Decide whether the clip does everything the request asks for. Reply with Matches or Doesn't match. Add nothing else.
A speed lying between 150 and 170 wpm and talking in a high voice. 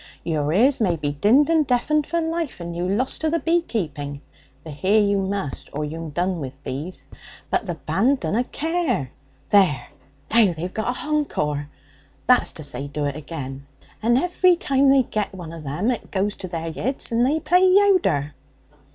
Doesn't match